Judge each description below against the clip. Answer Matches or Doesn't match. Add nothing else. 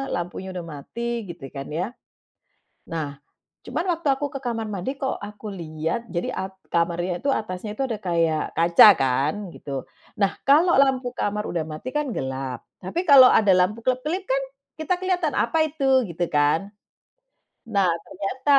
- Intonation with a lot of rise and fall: Matches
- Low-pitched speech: Doesn't match